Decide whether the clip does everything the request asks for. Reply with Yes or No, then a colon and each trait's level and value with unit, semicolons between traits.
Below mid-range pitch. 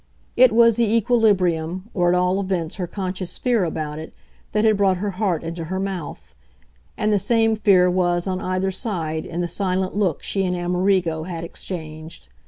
No: medium, 185 Hz